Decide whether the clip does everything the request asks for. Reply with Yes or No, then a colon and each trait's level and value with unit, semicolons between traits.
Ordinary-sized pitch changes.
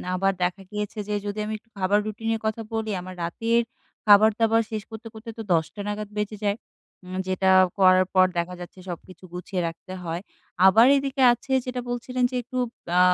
Yes: average, 3.3 semitones